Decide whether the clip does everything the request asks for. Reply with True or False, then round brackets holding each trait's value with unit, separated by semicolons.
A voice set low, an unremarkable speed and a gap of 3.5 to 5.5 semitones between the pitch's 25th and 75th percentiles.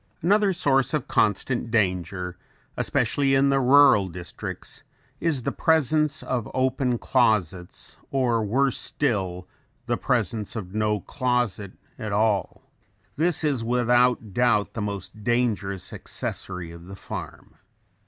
False (120 Hz; 125 wpm; 5.2 semitones)